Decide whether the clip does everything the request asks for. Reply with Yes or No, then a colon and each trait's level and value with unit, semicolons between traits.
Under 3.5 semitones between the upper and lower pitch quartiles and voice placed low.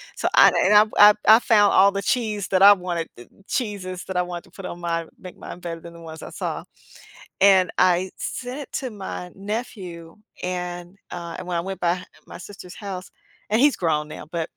No: average, 2.9 semitones; medium, 185 Hz